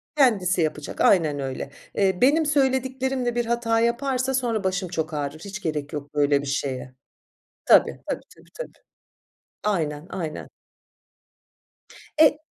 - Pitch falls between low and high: No, high, 195 Hz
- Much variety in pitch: Yes, wide, 8.9 semitones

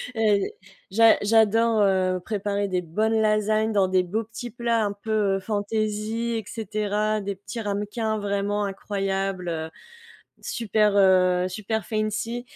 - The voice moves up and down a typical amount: No, narrow, 2.0 semitones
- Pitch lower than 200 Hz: No, high, 210 Hz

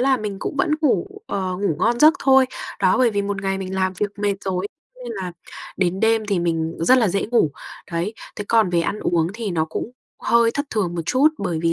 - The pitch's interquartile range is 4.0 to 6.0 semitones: Yes, average, 4.3 semitones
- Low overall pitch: No, high, 200 Hz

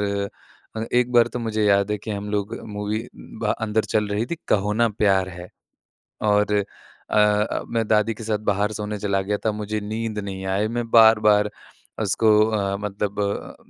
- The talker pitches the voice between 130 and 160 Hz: No, low, 105 Hz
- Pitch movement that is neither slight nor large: No, narrow, 1.3 semitones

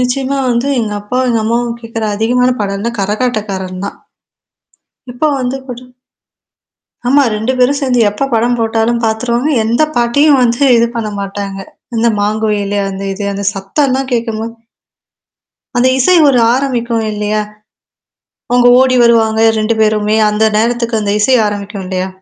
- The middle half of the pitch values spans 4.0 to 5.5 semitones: No, average, 2.9 semitones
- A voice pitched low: No, high, 230 Hz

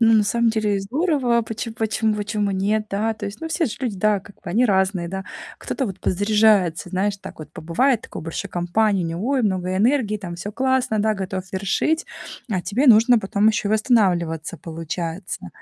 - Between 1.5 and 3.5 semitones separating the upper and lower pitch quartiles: Yes, average, 3.1 semitones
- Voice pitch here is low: No, high, 205 Hz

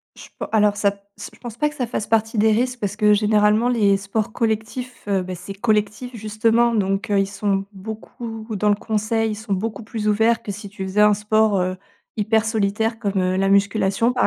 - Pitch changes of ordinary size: No, narrow, 1.9 semitones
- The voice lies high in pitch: Yes, high, 210 Hz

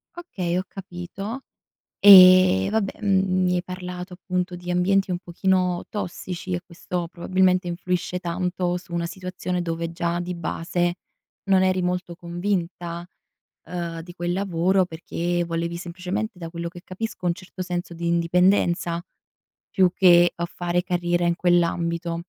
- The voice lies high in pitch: No, medium, 180 Hz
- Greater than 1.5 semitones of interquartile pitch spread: No, narrow, 1.2 semitones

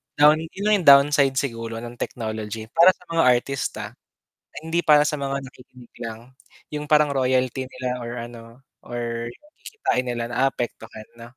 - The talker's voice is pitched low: Yes, low, 130 Hz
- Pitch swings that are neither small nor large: Yes, average, 3.7 semitones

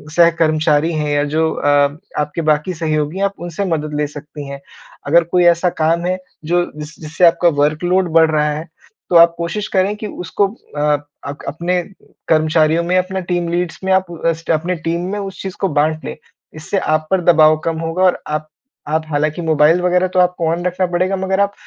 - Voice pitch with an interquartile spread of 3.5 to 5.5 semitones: No, average, 2.7 semitones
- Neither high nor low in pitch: Yes, medium, 165 Hz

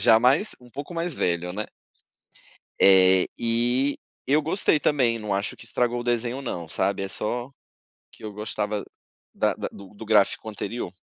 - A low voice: Yes, low, 115 Hz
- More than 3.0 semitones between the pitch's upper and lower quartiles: Yes, average, 3.8 semitones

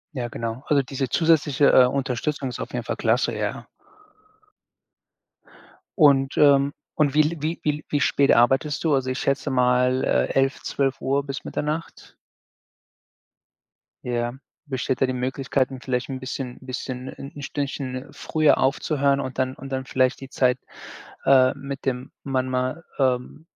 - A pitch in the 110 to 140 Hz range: Yes, low, 135 Hz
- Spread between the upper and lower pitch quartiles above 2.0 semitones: No, narrow, 1.6 semitones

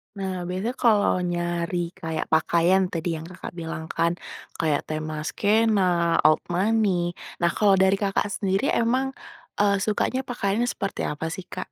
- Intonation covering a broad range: No, average, 3.6 semitones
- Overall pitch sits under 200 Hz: Yes, high, 190 Hz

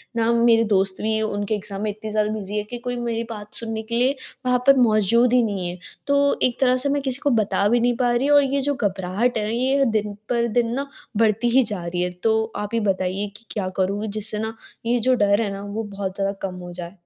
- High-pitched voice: Yes, high, 220 Hz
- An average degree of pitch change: Yes, average, 3.1 semitones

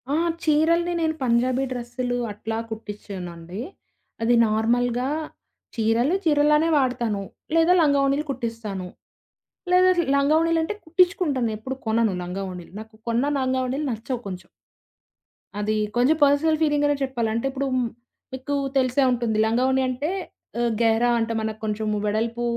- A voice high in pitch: Yes, high, 245 Hz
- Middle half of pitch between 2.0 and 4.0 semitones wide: No, average, 4.6 semitones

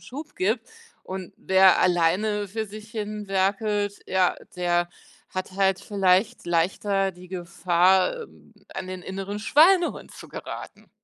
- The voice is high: Yes, high, 195 Hz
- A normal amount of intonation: No, narrow, 2.3 semitones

